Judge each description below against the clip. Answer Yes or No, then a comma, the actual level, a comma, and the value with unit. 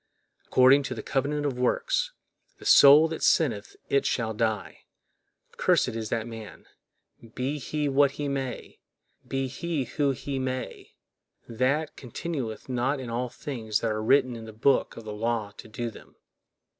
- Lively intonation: No, average, 3.7 semitones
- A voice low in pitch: Yes, low, 130 Hz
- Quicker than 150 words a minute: Yes, average, 160 wpm